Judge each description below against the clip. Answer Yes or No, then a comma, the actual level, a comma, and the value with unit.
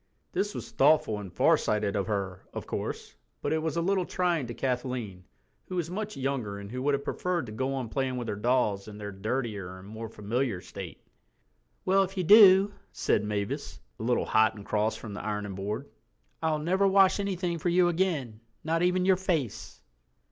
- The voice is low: Yes, low, 130 Hz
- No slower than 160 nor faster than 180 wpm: No, average, 195 wpm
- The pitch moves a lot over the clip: Yes, wide, 8.9 semitones